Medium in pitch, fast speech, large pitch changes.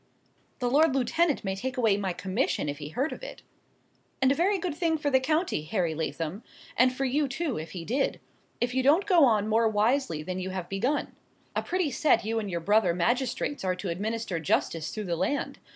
No: high, 230 Hz; fast, 210 wpm; wide, 7.1 semitones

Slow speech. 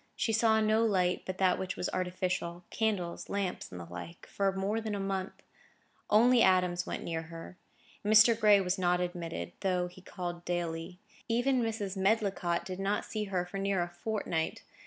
No: average, 170 wpm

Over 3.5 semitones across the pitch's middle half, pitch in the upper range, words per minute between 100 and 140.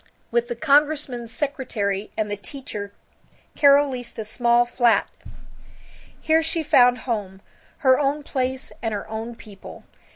Yes: average, 4.2 semitones; high, 245 Hz; slow, 135 wpm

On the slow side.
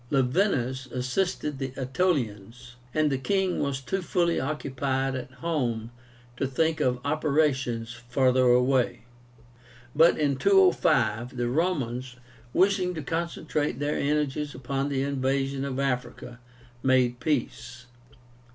Yes: slow, 115 wpm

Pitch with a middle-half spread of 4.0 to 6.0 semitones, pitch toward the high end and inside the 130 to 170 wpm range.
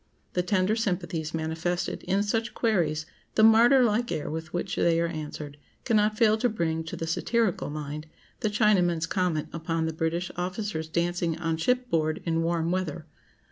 No: average, 4.6 semitones; medium, 175 Hz; average, 165 wpm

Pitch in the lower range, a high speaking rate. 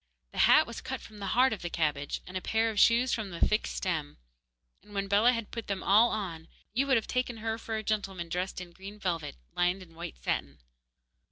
No: high, 200 Hz; fast, 230 wpm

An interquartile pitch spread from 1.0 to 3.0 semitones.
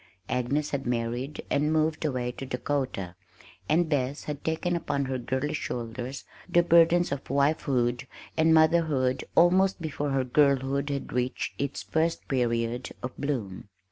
No: average, 3.7 semitones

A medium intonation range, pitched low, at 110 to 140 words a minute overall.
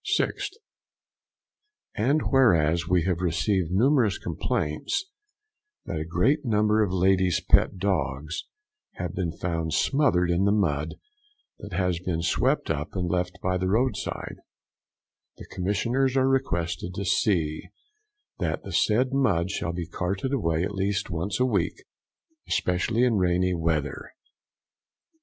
Yes: average, 3.9 semitones; very low, 90 Hz; slow, 135 wpm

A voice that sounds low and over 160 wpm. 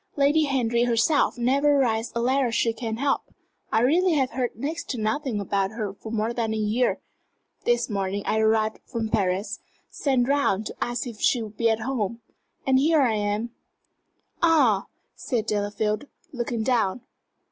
No: high, 235 Hz; average, 170 wpm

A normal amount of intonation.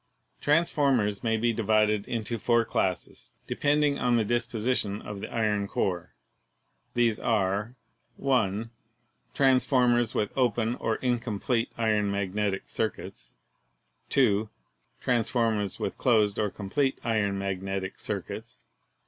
Yes: average, 3.0 semitones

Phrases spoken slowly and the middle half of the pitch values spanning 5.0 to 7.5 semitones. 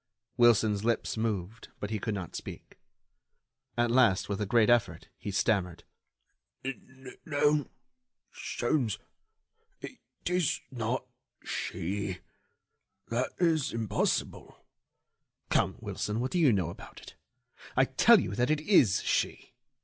No: slow, 120 wpm; average, 4.1 semitones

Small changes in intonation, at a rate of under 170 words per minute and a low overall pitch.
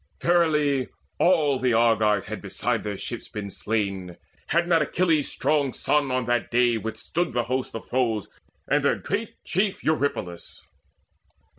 No: wide, 5.4 semitones; average, 145 wpm; low, 125 Hz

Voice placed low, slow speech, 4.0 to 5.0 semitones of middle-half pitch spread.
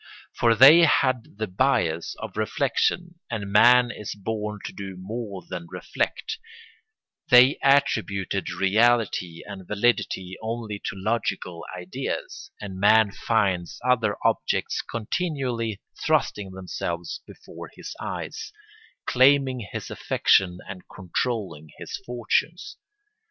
Yes: low, 105 Hz; slow, 110 wpm; average, 4.3 semitones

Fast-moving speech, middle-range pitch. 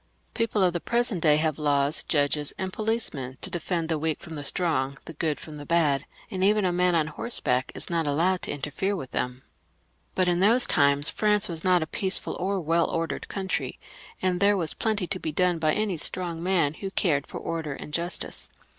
Yes: fast, 210 wpm; medium, 170 Hz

